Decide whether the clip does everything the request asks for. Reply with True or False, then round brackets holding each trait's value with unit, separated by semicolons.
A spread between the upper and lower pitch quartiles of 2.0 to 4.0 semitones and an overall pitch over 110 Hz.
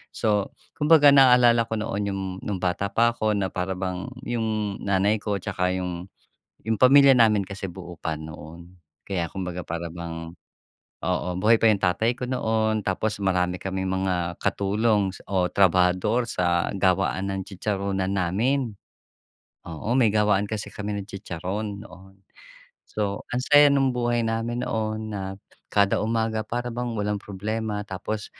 False (3.2 semitones; 100 Hz)